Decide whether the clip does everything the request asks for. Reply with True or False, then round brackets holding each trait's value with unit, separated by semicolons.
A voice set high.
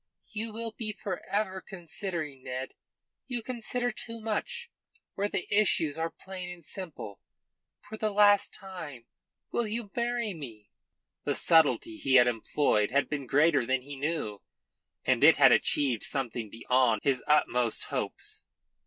False (170 Hz)